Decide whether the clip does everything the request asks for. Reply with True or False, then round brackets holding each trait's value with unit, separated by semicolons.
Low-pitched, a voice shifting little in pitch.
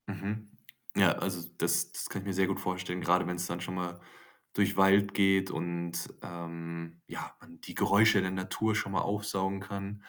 True (95 Hz; 2.1 semitones)